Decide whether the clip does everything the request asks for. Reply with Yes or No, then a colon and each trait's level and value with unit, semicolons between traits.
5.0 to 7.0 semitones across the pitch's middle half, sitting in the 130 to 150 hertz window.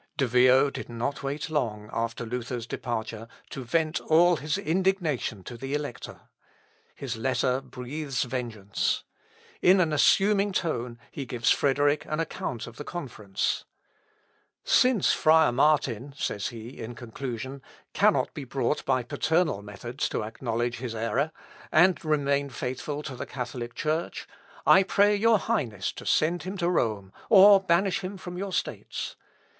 Yes: average, 5.3 semitones; low, 135 Hz